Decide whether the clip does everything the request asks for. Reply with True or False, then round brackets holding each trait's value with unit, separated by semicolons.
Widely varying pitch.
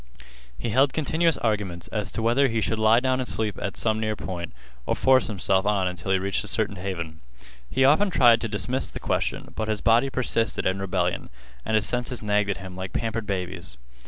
False (4.1 semitones)